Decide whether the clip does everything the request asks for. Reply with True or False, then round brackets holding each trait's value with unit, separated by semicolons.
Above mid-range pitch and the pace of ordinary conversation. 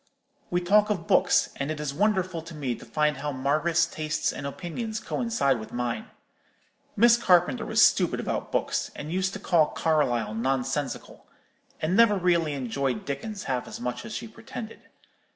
False (155 Hz; 170 wpm)